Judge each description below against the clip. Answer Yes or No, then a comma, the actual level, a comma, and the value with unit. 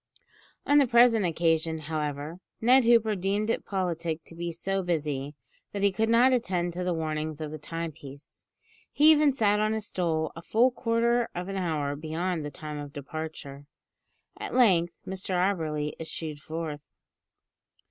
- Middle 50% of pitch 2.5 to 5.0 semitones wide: No, wide, 5.4 semitones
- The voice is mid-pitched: Yes, medium, 170 Hz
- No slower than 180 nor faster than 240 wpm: No, average, 160 wpm